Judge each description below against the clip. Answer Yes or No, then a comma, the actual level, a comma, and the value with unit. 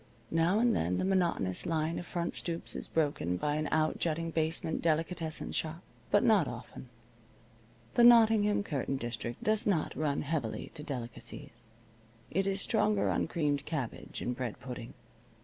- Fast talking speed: No, average, 150 wpm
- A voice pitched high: No, medium, 160 Hz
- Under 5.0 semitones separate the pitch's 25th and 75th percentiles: No, wide, 5.5 semitones